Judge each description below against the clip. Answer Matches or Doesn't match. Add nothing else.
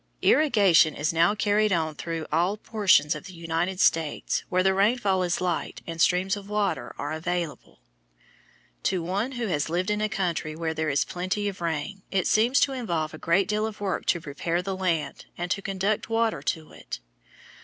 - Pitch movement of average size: Matches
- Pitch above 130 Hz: Matches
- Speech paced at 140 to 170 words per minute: Doesn't match